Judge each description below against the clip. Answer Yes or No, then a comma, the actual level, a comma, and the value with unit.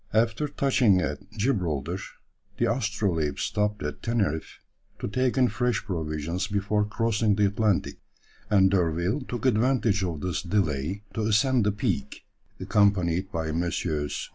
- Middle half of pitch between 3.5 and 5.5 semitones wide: Yes, average, 4.4 semitones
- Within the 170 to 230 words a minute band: No, slow, 135 wpm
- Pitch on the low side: Yes, low, 100 Hz